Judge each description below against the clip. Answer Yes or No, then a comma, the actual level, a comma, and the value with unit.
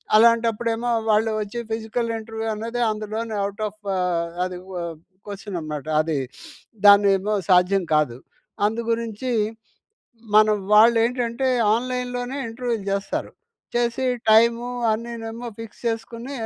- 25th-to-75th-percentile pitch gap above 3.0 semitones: No, narrow, 2.5 semitones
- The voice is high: Yes, high, 225 Hz